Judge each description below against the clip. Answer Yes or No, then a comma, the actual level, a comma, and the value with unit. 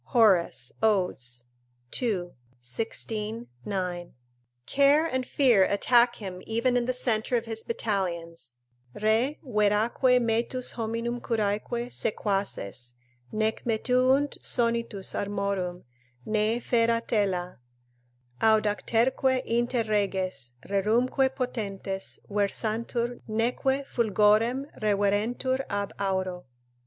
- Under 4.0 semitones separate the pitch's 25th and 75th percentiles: Yes, average, 3.3 semitones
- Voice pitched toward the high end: Yes, high, 220 Hz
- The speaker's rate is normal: No, slow, 90 wpm